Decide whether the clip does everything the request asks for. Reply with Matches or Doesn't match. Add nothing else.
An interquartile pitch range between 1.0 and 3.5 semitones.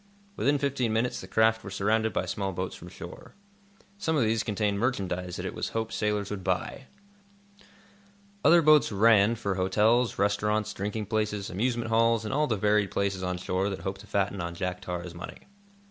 Matches